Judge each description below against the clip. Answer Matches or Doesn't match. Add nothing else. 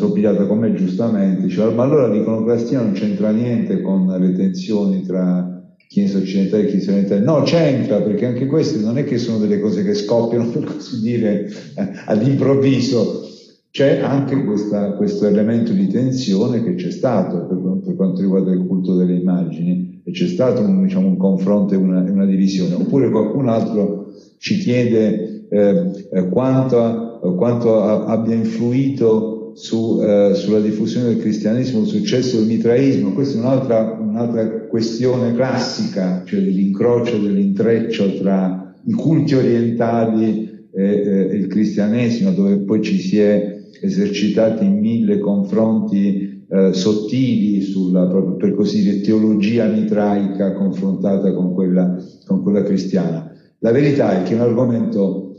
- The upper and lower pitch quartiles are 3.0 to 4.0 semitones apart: Matches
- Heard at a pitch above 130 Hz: Doesn't match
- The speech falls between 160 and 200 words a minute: Doesn't match